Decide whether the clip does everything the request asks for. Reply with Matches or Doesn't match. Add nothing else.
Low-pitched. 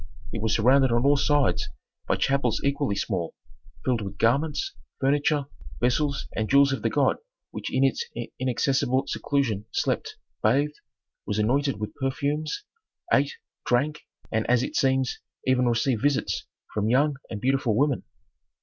Matches